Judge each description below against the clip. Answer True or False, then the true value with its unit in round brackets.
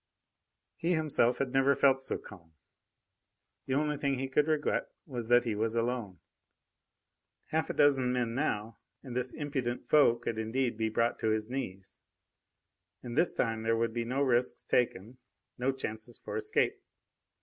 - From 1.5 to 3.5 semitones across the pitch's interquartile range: True (3.2 semitones)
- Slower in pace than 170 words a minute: True (160 wpm)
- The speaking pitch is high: False (125 Hz)